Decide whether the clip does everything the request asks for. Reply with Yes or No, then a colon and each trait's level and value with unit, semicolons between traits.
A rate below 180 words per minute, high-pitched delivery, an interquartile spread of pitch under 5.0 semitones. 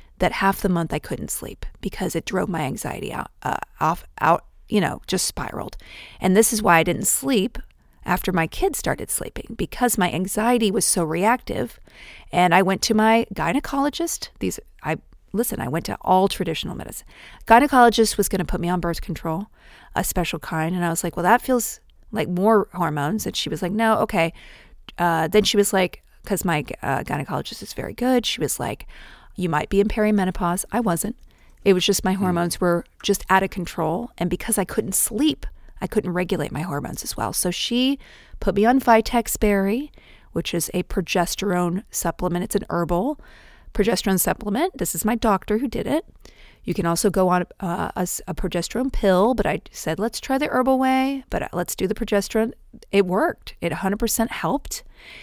No: average, 190 wpm; high, 195 Hz; average, 4.1 semitones